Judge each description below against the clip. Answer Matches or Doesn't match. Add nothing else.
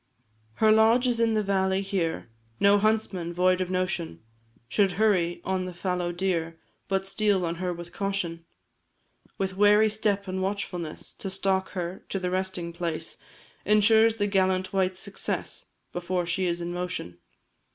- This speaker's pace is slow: Doesn't match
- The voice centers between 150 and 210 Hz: Matches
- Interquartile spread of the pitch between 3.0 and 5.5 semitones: Doesn't match